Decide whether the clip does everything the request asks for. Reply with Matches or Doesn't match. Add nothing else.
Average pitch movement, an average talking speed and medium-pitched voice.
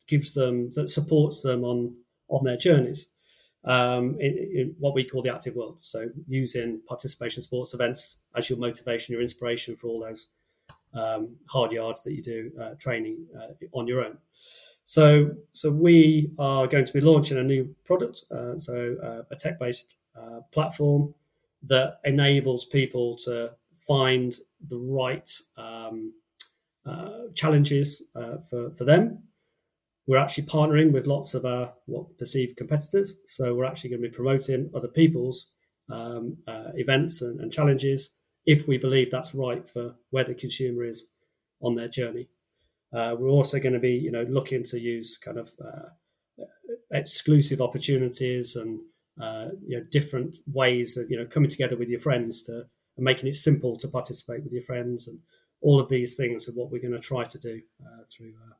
Doesn't match